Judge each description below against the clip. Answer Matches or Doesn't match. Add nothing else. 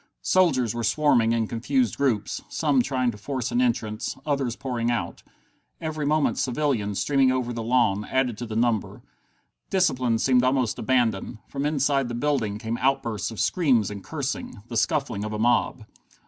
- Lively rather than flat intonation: Doesn't match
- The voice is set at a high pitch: Doesn't match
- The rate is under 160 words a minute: Doesn't match